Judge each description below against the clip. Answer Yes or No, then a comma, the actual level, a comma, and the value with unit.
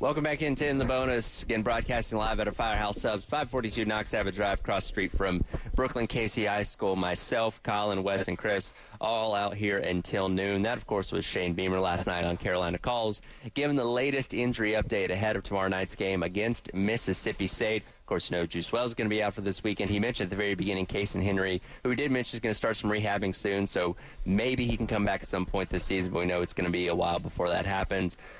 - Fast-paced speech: Yes, fast, 245 wpm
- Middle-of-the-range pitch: No, low, 105 Hz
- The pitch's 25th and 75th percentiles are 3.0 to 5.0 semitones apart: Yes, average, 3.6 semitones